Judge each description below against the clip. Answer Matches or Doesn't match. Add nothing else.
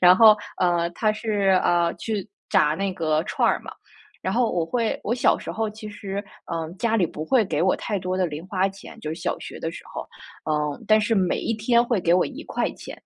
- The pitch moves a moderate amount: Matches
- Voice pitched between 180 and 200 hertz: Matches